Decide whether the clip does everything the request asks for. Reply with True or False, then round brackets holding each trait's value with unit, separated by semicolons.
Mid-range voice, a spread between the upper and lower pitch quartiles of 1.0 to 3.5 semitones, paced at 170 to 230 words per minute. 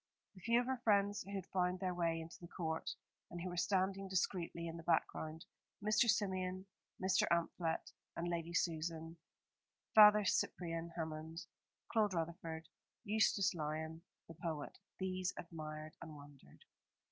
False (170 Hz; 2.8 semitones; 145 wpm)